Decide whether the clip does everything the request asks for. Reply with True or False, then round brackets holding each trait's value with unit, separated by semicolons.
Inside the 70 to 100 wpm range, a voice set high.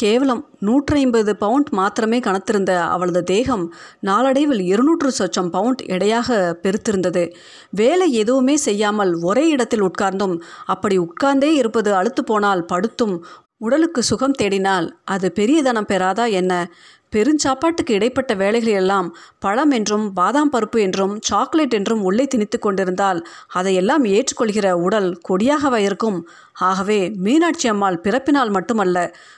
False (115 wpm; 210 Hz)